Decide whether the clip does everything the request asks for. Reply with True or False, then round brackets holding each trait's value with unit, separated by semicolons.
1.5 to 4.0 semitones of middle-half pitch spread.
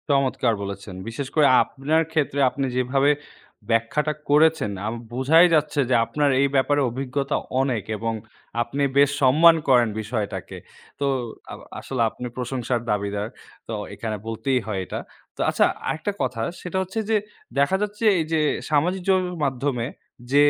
False (4.5 semitones)